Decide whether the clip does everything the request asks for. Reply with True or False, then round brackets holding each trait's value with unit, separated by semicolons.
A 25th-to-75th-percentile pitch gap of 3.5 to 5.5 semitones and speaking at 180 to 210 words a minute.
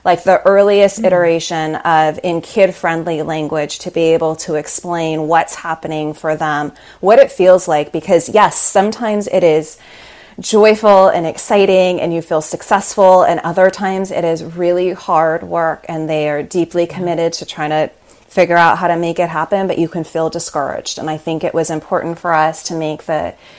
False (2.6 semitones; 185 wpm)